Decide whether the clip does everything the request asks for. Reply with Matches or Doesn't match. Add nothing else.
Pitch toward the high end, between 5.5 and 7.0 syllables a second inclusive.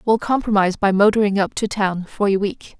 Matches